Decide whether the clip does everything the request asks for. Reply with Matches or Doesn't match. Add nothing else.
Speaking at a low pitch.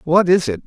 Doesn't match